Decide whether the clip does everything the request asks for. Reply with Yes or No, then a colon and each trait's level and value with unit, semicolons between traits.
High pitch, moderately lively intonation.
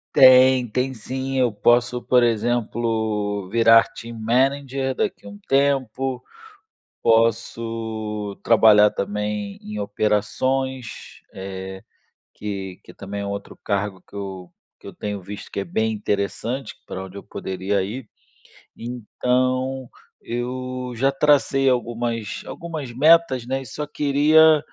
No: low, 115 Hz; average, 4.1 semitones